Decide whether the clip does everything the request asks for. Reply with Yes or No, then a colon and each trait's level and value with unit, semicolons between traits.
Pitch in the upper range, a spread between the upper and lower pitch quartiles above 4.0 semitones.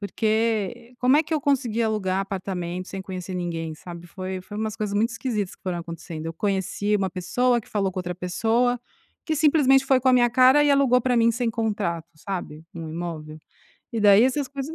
Yes: high, 210 Hz; wide, 5.4 semitones